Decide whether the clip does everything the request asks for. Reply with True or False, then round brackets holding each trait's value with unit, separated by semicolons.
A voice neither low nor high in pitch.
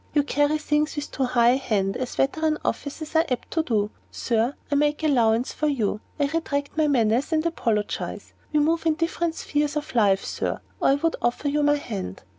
False (285 Hz)